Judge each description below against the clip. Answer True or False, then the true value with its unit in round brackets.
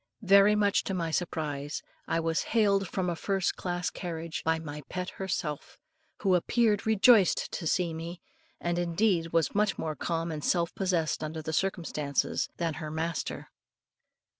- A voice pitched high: False (170 Hz)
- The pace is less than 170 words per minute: True (160 wpm)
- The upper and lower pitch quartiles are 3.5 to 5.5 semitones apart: False (3.1 semitones)